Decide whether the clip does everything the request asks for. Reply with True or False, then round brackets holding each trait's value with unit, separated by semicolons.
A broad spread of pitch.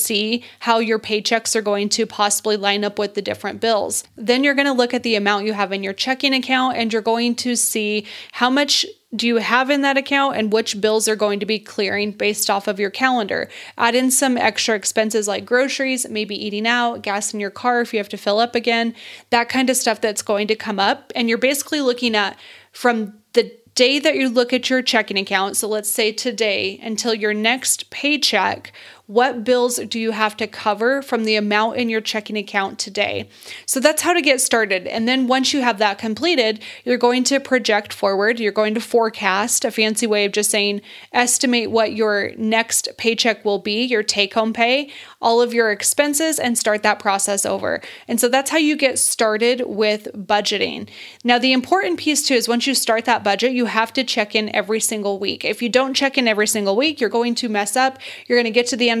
False (2.9 semitones)